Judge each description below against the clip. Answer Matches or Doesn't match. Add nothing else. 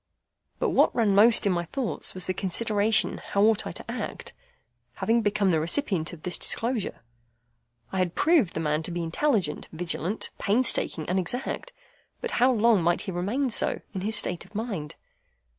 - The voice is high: Matches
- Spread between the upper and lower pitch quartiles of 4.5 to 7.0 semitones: Matches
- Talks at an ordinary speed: Matches